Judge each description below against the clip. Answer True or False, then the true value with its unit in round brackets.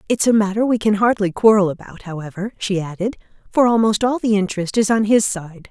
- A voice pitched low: False (205 Hz)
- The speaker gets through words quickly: True (210 wpm)